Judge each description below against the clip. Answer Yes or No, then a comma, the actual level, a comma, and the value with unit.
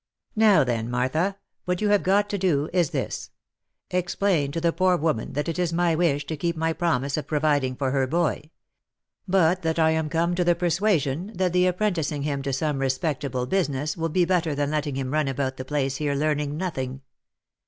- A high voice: No, medium, 155 Hz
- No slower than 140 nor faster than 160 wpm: No, fast, 205 wpm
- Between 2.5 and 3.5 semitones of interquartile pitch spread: No, average, 4.0 semitones